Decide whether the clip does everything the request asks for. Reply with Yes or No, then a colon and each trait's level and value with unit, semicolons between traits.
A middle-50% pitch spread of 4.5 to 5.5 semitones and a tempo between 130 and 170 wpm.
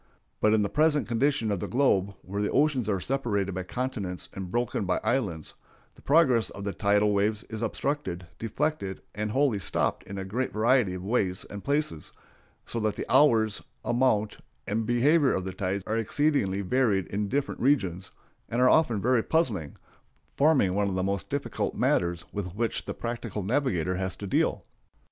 No: average, 5.1 semitones; average, 180 wpm